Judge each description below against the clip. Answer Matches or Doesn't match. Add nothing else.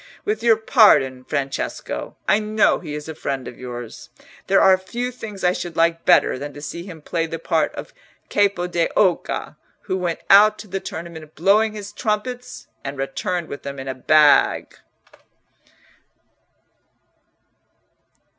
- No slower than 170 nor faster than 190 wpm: Doesn't match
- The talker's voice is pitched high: Doesn't match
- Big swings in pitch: Matches